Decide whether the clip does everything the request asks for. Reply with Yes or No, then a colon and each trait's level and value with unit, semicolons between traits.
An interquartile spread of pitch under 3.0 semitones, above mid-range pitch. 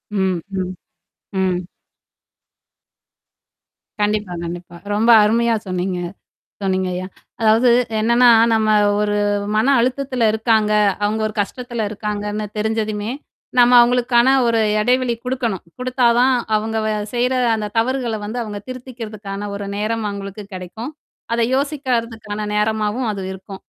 Yes: narrow, 2.6 semitones; high, 220 Hz